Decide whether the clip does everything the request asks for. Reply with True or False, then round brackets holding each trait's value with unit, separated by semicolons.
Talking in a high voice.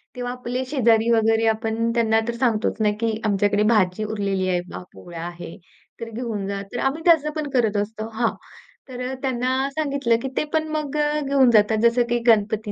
True (230 Hz)